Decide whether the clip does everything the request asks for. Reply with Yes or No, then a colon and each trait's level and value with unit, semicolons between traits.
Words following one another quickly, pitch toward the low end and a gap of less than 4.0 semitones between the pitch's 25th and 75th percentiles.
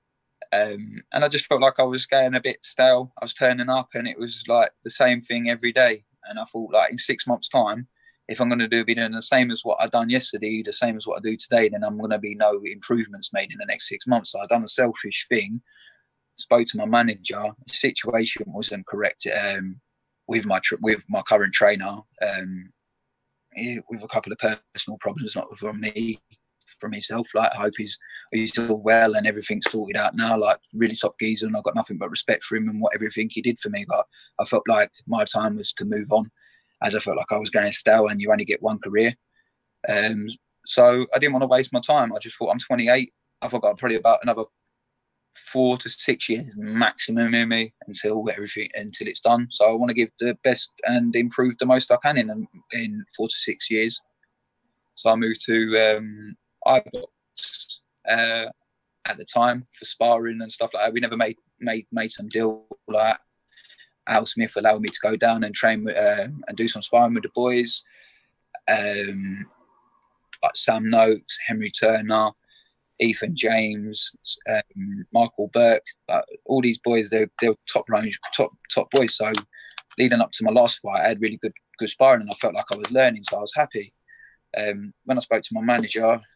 Yes: fast, 210 wpm; low, 115 Hz; narrow, 2.6 semitones